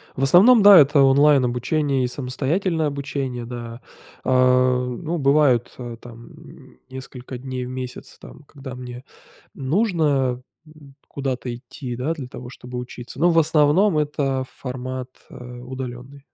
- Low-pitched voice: Yes, low, 130 Hz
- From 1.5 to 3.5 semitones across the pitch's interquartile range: Yes, average, 2.8 semitones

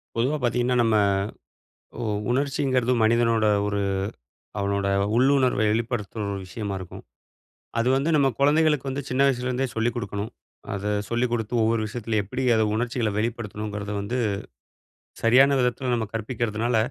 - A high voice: No, low, 115 Hz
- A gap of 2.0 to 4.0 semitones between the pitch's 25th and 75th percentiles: Yes, average, 2.9 semitones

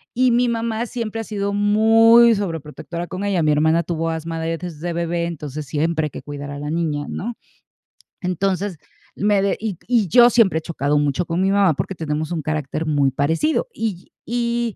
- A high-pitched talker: No, medium, 175 Hz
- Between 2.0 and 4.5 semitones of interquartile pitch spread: No, wide, 5.5 semitones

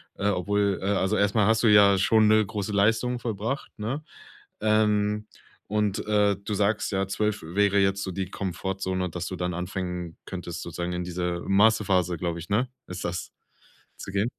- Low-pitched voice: Yes, low, 100 Hz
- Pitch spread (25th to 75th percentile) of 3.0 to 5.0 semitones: No, narrow, 2.6 semitones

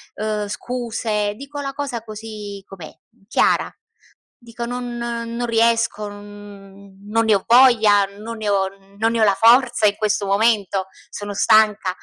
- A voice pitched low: No, high, 215 Hz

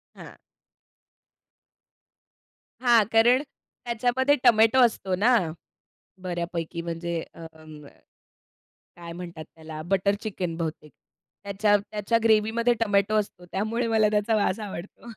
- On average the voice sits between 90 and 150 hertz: No, high, 205 Hz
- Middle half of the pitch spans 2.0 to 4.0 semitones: No, average, 4.7 semitones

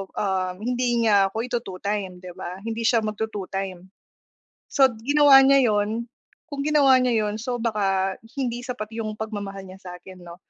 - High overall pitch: Yes, high, 215 Hz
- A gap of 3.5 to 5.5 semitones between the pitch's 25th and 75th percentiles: Yes, average, 4.0 semitones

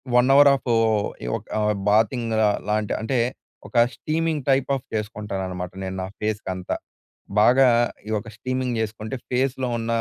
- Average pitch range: Yes, average, 3.8 semitones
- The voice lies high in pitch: No, low, 115 Hz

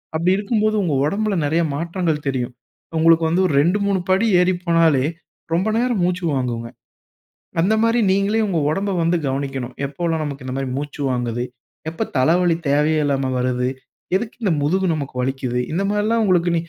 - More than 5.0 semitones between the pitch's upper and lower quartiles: Yes, wide, 5.6 semitones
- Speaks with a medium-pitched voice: Yes, medium, 165 Hz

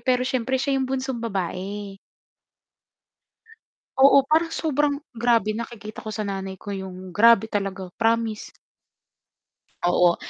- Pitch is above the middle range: Yes, high, 225 Hz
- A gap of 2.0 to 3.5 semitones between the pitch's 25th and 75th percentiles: No, average, 4.9 semitones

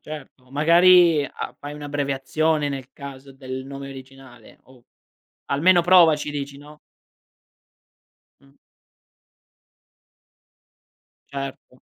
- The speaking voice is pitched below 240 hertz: Yes, medium, 140 Hz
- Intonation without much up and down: Yes, narrow, 2.2 semitones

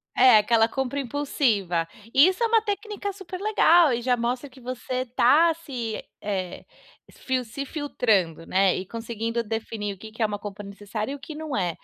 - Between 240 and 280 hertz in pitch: Yes, high, 245 Hz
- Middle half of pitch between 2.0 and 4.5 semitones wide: No, wide, 5.5 semitones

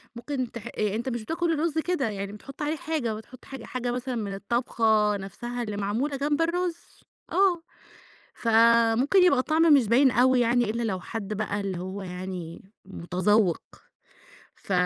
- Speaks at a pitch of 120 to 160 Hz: No, high, 235 Hz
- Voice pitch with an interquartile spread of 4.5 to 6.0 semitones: Yes, average, 5.2 semitones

